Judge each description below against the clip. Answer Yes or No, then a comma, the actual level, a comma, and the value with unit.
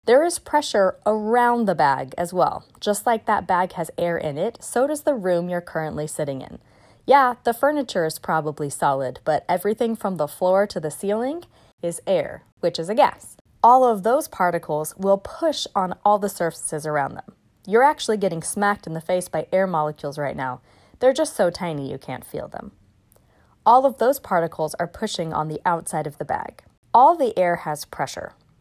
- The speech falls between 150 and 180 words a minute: No, average, 195 wpm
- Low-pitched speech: No, medium, 180 Hz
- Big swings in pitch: Yes, wide, 6.7 semitones